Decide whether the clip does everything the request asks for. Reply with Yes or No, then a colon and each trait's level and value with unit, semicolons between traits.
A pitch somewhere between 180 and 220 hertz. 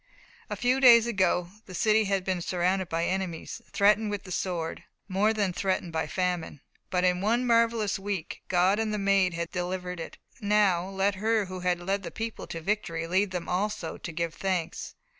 Yes: high, 190 Hz